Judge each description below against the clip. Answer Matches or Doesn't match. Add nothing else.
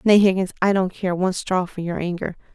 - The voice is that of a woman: Matches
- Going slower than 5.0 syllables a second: Doesn't match